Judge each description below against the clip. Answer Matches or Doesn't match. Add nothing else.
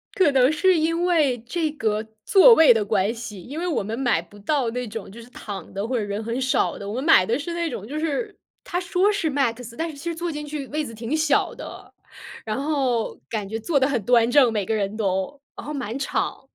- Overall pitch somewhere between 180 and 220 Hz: Doesn't match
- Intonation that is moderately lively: Doesn't match